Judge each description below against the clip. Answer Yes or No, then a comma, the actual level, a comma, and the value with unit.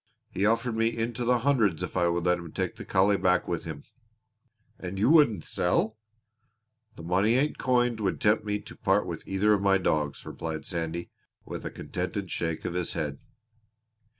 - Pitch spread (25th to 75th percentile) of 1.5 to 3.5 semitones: No, average, 4.6 semitones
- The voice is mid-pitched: No, very low, 95 Hz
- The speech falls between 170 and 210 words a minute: Yes, average, 185 wpm